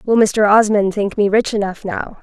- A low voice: No, high, 205 Hz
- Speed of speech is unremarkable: No, fast, 215 wpm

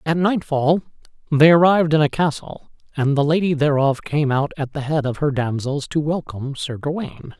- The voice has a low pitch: No, medium, 150 Hz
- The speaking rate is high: No, average, 185 wpm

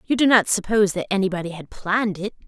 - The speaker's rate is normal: No, fast, 220 wpm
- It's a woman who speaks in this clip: Yes, female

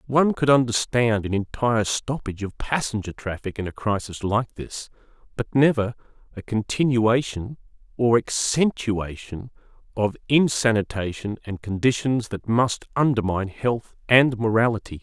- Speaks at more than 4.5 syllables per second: Yes, 4.7 syllables/s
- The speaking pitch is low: Yes, low, 115 Hz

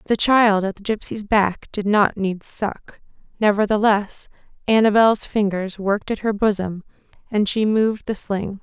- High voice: Yes, high, 205 Hz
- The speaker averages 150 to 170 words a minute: Yes, average, 155 wpm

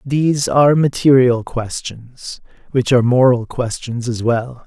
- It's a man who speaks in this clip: Yes, male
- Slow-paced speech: Yes, slow, 130 wpm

